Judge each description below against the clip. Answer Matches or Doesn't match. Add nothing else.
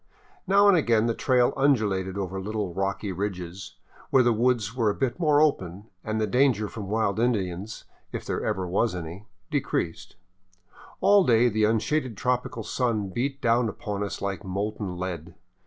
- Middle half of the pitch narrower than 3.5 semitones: Doesn't match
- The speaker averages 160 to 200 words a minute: Matches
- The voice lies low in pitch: Matches